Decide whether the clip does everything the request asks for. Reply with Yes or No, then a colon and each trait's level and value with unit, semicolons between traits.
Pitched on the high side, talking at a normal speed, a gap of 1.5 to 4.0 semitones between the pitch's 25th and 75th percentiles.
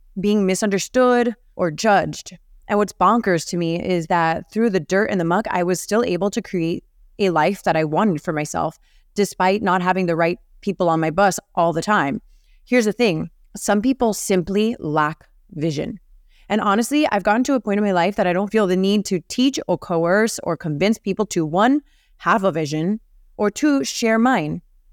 Yes: high, 195 Hz; average, 195 wpm; average, 3.7 semitones